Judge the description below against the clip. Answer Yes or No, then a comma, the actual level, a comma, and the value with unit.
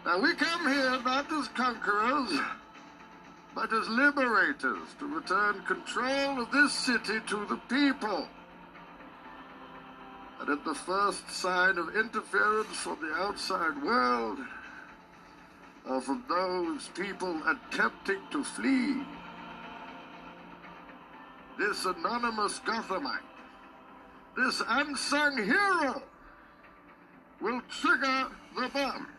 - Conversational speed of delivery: No, slow, 95 wpm